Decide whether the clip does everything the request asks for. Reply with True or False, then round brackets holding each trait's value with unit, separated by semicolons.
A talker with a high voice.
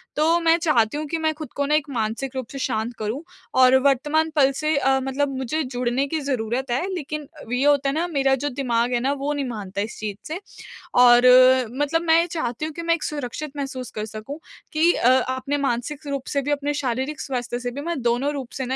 True (275 Hz)